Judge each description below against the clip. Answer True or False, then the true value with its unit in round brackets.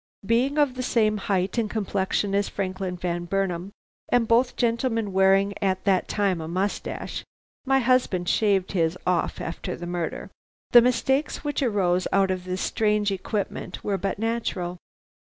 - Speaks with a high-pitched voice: True (200 Hz)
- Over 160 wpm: False (155 wpm)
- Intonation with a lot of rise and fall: False (3.8 semitones)